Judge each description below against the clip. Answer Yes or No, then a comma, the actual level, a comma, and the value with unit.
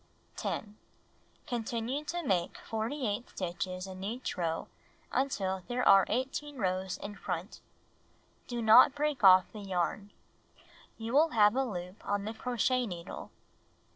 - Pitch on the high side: Yes, high, 215 Hz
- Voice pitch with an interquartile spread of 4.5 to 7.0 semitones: Yes, average, 4.9 semitones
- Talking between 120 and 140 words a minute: Yes, slow, 135 wpm